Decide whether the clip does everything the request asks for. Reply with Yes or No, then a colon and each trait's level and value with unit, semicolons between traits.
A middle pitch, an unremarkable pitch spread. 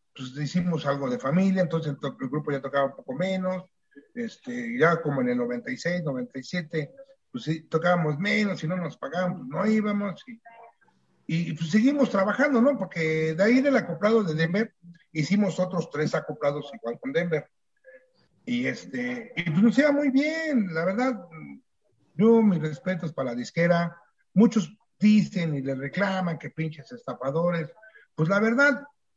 No: medium, 180 Hz; wide, 6.2 semitones